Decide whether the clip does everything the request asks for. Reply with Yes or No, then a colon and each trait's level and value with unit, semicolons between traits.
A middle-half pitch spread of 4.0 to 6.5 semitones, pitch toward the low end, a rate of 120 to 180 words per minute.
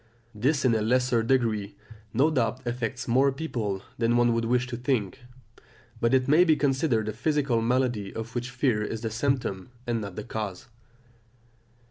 No: average, 2.9 semitones; low, 120 Hz; average, 170 wpm